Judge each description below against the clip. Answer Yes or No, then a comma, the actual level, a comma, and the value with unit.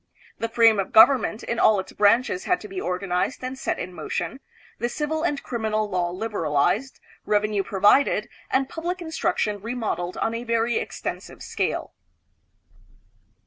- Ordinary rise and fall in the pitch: Yes, average, 4.7 semitones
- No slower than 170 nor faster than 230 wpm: No, average, 155 wpm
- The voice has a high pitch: Yes, high, 225 Hz